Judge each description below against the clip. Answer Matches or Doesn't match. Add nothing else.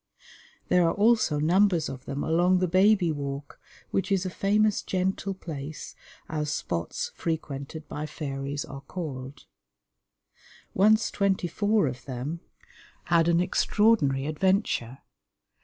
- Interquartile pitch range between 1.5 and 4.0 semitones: Doesn't match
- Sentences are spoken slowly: Matches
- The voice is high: Doesn't match